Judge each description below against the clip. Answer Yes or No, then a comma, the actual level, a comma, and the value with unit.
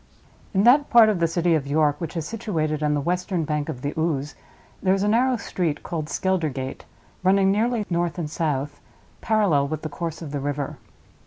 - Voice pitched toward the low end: No, medium, 165 Hz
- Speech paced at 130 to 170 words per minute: No, average, 195 wpm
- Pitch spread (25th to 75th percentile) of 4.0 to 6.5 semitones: Yes, average, 4.5 semitones